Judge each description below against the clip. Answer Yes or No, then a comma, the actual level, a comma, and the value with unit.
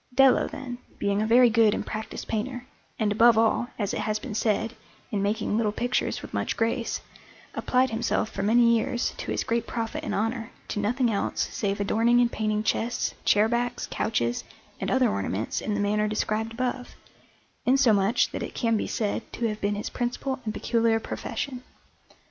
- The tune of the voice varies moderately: No, narrow, 2.3 semitones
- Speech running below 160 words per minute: No, average, 185 wpm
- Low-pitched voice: No, high, 225 Hz